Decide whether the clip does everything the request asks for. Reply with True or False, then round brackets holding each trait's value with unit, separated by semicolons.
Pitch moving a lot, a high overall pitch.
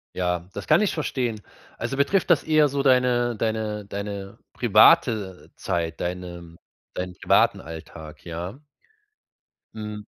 False (6.1 semitones; 105 Hz)